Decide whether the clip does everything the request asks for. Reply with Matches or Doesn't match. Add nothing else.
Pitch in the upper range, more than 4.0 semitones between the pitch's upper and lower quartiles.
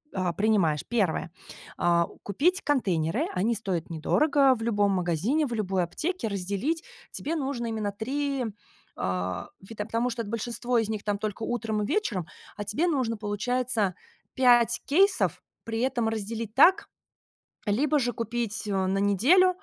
Matches